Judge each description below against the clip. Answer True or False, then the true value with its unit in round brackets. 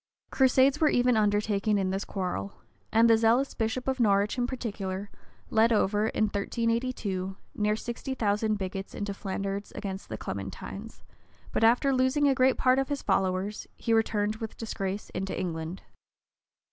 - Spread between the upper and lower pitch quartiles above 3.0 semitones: True (3.7 semitones)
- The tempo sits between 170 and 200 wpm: False (155 wpm)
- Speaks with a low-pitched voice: False (215 Hz)